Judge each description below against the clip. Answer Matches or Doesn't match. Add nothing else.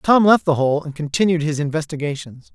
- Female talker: Doesn't match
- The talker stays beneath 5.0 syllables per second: Doesn't match